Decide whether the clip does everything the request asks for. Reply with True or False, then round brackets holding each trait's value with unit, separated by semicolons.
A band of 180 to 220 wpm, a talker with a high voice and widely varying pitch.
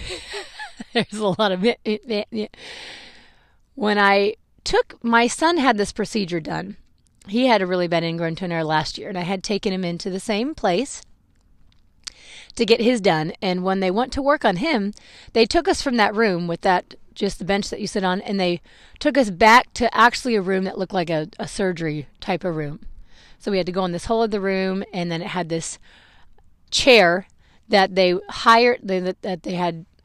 False (205 wpm; 200 Hz; 4.0 semitones)